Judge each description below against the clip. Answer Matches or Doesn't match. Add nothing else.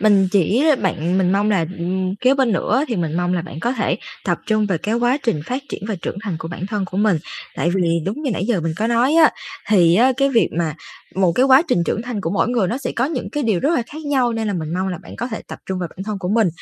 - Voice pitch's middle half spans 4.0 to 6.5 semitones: Matches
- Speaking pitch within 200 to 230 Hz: Matches